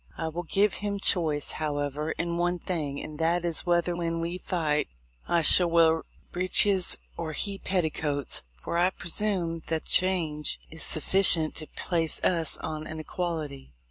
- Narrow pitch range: Yes, narrow, 2.3 semitones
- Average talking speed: Yes, average, 160 wpm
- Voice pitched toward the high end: No, medium, 165 Hz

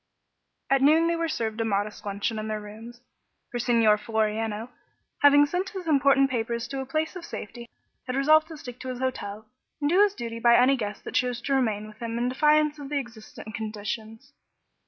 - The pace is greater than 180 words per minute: Yes, average, 200 wpm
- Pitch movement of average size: Yes, average, 4.7 semitones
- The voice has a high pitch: Yes, high, 240 Hz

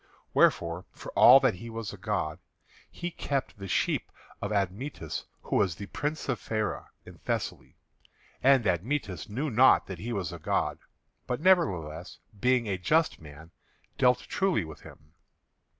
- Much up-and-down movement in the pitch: Yes, wide, 6.9 semitones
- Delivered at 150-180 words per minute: Yes, average, 155 wpm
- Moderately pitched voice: No, low, 105 Hz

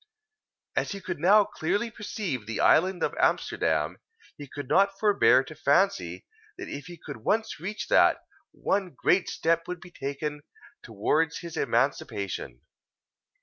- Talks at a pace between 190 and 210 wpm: No, average, 145 wpm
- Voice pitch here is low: No, medium, 170 Hz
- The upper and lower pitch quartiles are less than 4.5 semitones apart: No, wide, 5.6 semitones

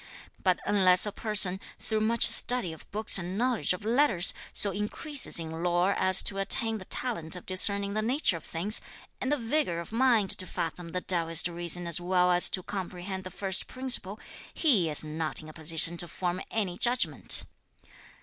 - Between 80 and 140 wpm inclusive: No, average, 185 wpm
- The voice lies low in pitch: No, medium, 185 Hz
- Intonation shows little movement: No, average, 3.8 semitones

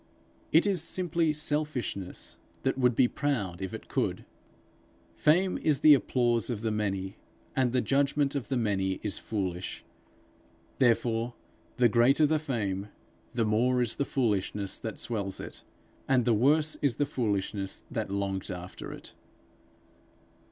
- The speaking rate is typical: Yes, average, 145 wpm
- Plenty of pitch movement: Yes, wide, 5.7 semitones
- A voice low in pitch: Yes, low, 120 Hz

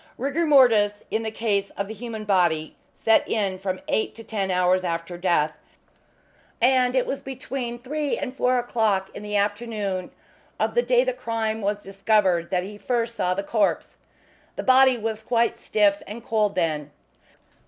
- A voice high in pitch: Yes, high, 215 Hz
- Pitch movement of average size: Yes, average, 3.9 semitones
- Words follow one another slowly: No, average, 170 wpm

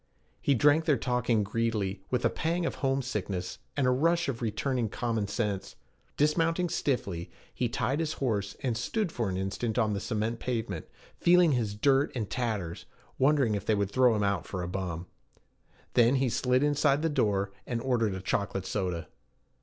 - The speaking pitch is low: Yes, low, 115 Hz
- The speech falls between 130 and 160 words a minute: No, average, 180 wpm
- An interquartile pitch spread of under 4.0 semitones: No, average, 5.2 semitones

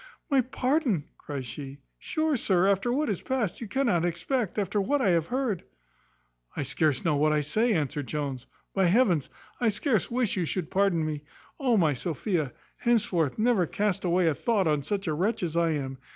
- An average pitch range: No, wide, 7.0 semitones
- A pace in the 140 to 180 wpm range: No, average, 190 wpm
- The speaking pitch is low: No, medium, 185 Hz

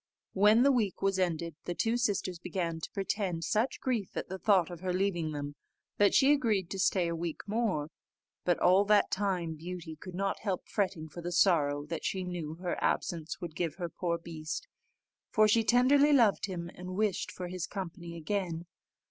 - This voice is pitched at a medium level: Yes, medium, 180 Hz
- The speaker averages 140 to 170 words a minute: No, average, 195 wpm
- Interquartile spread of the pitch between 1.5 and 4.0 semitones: Yes, average, 3.3 semitones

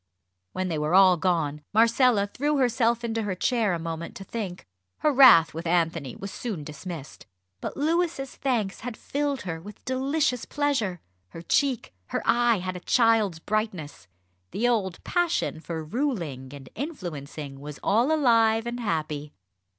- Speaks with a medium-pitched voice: No, high, 205 Hz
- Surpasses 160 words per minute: No, average, 155 wpm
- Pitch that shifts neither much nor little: No, wide, 7.0 semitones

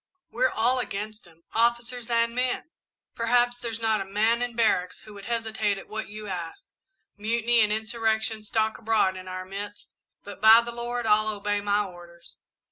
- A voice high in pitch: Yes, high, 220 Hz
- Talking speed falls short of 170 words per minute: No, average, 175 wpm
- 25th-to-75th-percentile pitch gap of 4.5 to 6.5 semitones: No, narrow, 2.4 semitones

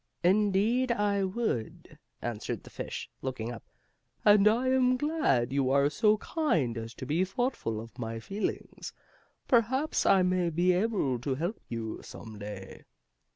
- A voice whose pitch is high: No, medium, 180 Hz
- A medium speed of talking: Yes, average, 150 wpm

